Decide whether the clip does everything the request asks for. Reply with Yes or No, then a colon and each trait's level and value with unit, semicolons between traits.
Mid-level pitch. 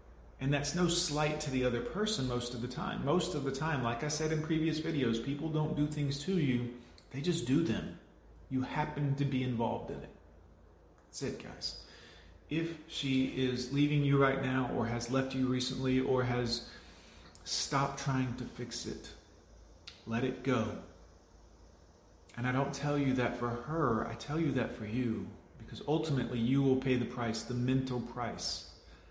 No: low, 125 Hz